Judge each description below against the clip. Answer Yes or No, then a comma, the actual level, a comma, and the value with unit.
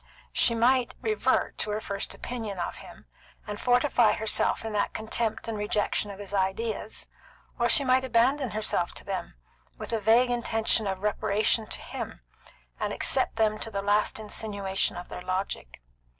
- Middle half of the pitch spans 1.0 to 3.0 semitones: Yes, narrow, 2.5 semitones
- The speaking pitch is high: Yes, high, 215 Hz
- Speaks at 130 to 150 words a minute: No, average, 165 wpm